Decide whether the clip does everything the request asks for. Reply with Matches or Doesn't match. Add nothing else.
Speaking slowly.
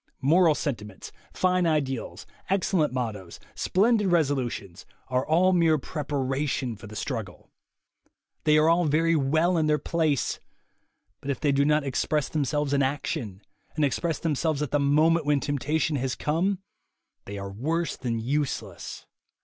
Doesn't match